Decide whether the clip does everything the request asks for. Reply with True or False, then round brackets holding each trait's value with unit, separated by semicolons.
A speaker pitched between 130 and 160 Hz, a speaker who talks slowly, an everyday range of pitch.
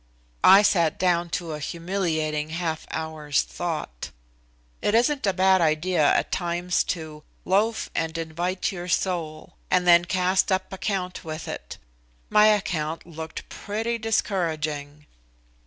False (175 Hz; 130 wpm; 3.1 semitones)